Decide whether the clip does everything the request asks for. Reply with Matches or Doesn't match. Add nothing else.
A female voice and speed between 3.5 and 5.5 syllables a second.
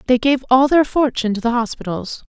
Doesn't match